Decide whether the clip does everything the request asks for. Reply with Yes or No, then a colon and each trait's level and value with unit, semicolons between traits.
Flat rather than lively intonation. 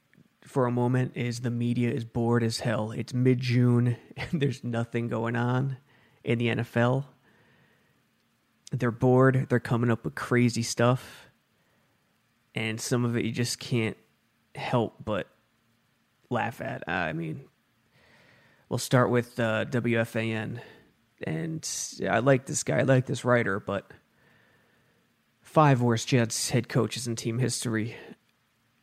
Yes: narrow, 1.7 semitones